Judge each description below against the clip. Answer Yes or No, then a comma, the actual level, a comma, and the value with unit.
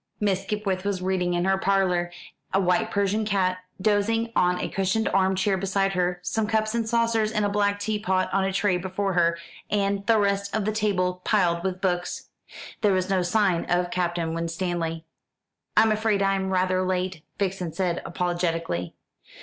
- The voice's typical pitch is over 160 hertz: Yes, high, 190 Hz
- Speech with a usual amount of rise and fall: No, narrow, 2.2 semitones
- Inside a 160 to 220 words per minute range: Yes, average, 175 wpm